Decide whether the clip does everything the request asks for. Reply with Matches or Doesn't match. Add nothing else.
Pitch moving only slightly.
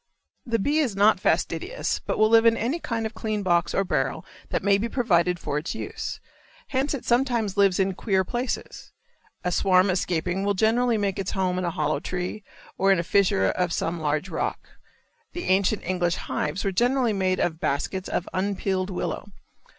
Doesn't match